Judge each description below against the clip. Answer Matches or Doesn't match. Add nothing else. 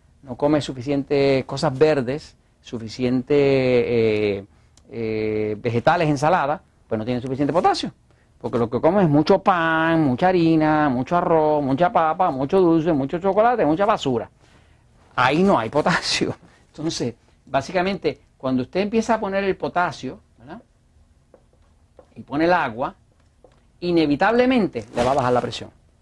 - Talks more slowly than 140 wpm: Matches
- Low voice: Doesn't match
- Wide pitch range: Matches